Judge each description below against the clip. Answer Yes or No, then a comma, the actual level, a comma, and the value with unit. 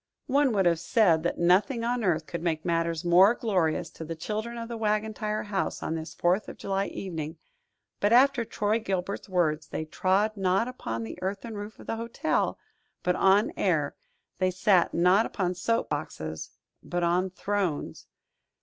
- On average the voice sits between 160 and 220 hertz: Yes, high, 190 Hz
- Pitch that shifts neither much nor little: Yes, average, 4.1 semitones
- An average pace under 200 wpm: Yes, average, 175 wpm